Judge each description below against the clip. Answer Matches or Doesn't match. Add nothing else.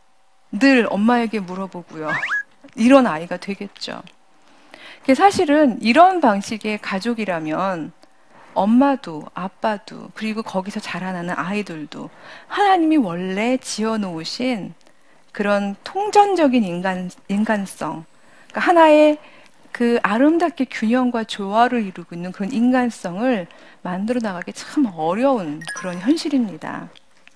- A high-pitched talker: Matches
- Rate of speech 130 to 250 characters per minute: Doesn't match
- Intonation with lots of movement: Matches